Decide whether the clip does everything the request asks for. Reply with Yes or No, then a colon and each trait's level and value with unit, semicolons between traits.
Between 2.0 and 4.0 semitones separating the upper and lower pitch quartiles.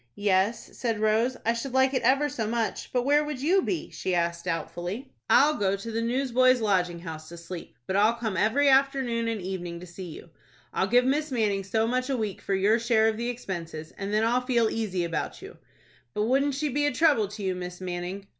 No: average, 5.3 semitones